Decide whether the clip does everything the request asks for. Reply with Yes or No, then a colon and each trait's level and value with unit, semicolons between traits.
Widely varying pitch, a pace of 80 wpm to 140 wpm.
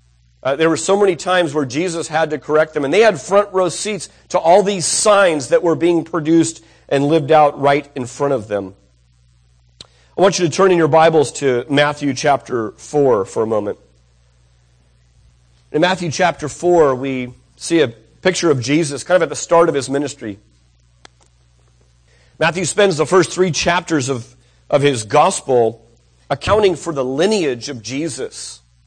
No: wide, 8.7 semitones; average, 175 wpm